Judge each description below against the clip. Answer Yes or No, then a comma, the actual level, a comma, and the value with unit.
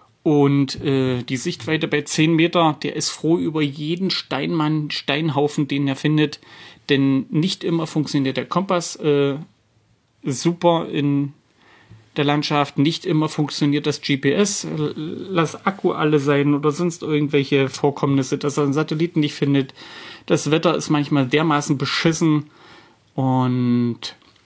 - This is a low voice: No, medium, 150 Hz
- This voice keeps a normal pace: Yes, average, 135 wpm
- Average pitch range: No, narrow, 2.2 semitones